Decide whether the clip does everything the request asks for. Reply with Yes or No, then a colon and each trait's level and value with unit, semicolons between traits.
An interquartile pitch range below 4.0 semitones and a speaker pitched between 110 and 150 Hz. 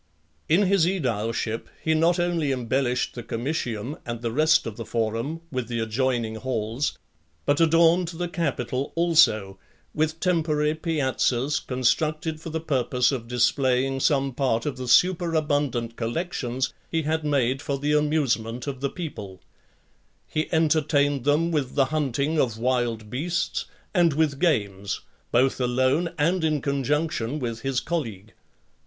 No: average, 4.7 semitones; medium, 140 Hz